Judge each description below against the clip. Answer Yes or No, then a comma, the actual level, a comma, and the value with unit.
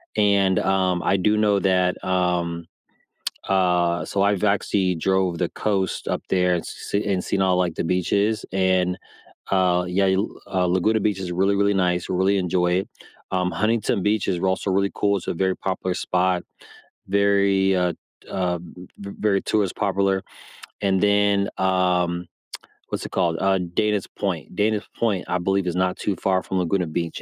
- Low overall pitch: Yes, very low, 95 Hz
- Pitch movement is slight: Yes, narrow, 1.6 semitones